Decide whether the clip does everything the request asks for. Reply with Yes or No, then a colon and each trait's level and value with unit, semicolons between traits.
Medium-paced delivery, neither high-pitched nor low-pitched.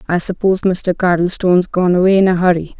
Yes: average, 195 wpm; medium, 180 Hz